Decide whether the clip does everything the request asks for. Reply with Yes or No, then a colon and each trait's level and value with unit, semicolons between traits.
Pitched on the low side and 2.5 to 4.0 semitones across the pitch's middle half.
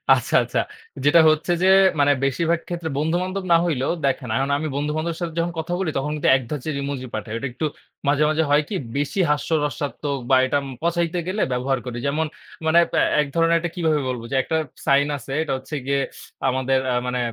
No: medium, 150 Hz; average, 3.5 semitones